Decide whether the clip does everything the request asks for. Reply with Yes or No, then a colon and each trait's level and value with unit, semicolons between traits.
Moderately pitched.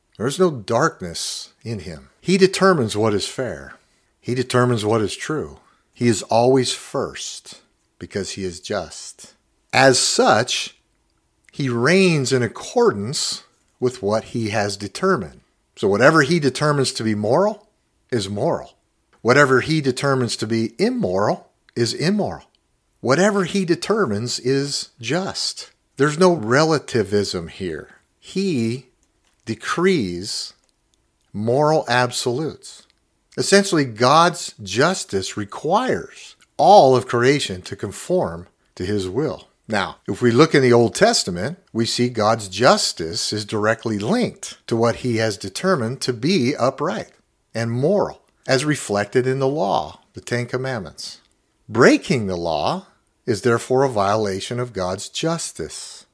No: low, 125 Hz